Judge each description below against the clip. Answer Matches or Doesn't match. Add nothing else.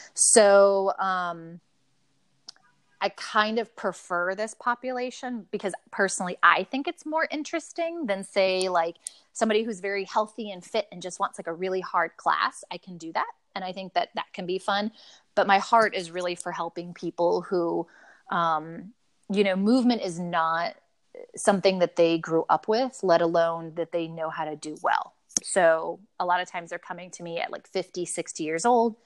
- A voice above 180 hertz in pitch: Matches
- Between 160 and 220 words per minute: Matches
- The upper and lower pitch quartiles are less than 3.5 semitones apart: Doesn't match